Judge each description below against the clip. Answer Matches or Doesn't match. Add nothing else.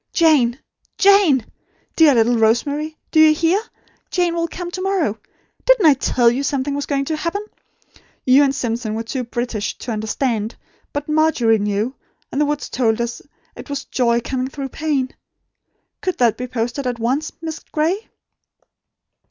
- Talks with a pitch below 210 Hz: Doesn't match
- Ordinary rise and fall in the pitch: Matches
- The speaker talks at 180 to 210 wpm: Doesn't match